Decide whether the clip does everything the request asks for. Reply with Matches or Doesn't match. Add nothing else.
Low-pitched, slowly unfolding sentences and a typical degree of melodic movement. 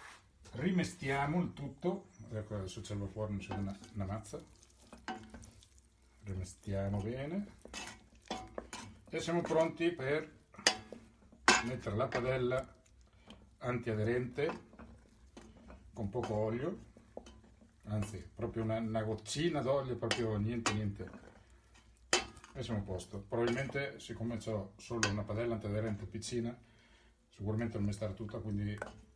Matches